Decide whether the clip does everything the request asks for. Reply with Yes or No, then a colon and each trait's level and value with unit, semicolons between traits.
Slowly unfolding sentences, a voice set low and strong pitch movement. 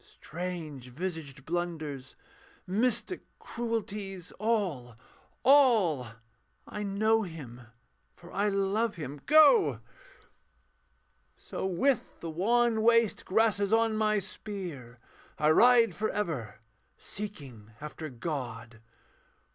No: slow, 95 wpm; high, 190 Hz; wide, 6.9 semitones